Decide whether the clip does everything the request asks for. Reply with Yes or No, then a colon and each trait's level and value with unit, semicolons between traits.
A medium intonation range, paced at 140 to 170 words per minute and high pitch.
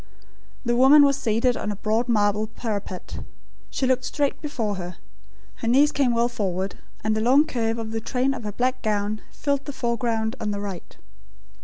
No: average, 3.5 semitones; average, 185 wpm; high, 230 Hz